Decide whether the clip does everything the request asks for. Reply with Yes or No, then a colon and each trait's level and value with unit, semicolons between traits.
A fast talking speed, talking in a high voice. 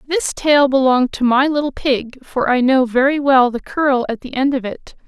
Yes: fast, 225 wpm; very high, 265 Hz